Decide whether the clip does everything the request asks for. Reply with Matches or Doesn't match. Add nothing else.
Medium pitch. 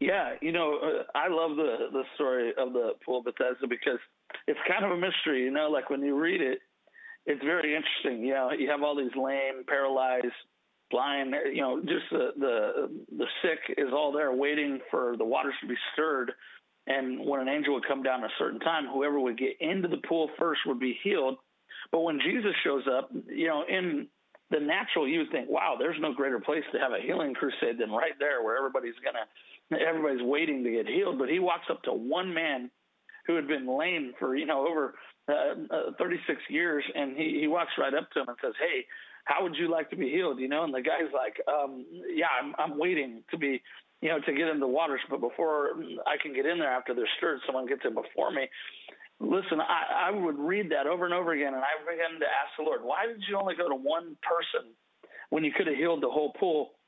Matches